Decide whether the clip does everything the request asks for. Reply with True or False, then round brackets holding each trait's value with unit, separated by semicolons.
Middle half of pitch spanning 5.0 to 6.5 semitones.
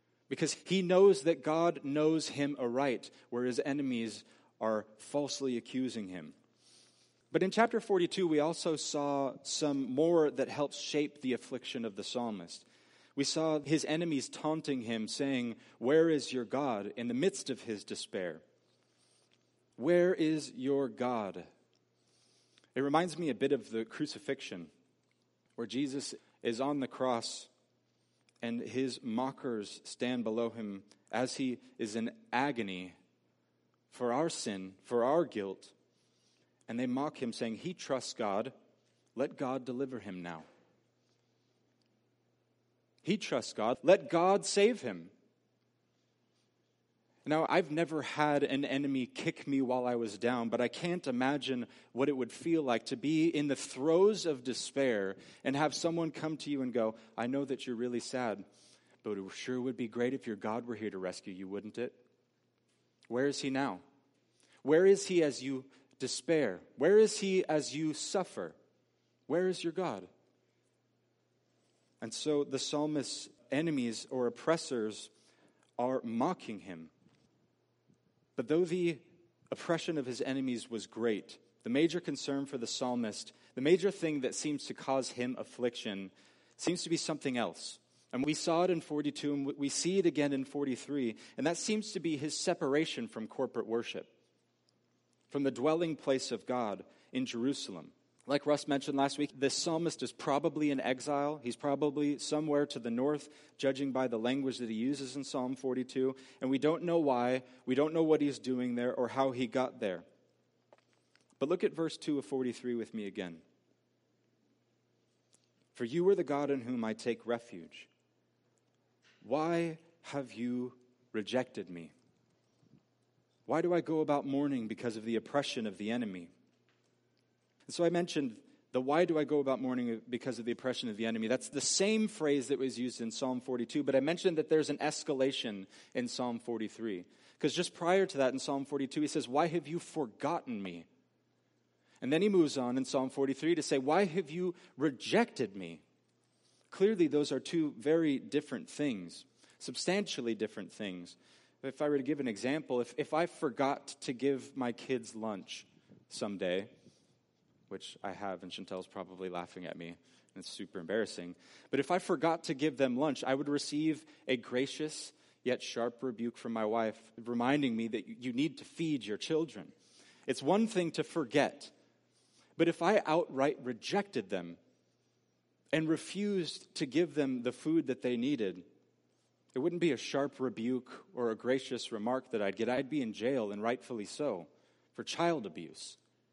False (4.4 semitones)